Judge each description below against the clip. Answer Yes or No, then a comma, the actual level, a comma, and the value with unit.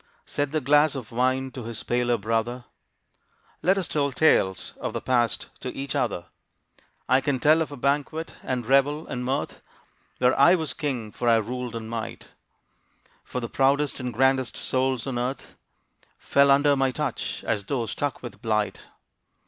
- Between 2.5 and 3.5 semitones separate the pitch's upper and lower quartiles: Yes, average, 2.9 semitones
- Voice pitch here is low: Yes, low, 130 Hz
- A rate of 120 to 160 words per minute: No, average, 170 wpm